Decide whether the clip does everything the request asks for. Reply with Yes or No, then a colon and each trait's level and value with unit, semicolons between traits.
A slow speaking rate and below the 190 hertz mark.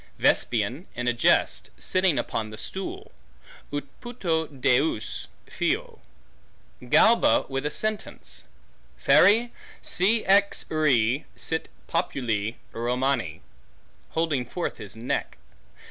Yes: slow, 100 wpm; medium, 140 Hz